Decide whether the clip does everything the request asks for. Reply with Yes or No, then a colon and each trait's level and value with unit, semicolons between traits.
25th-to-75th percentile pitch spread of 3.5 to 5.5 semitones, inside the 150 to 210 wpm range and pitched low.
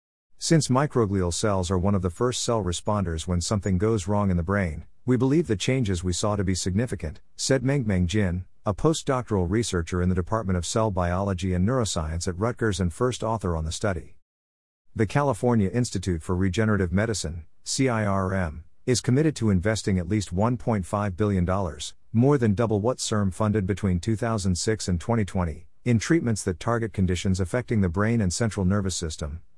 Yes: average, 4.0 semitones; average, 170 wpm; low, 100 Hz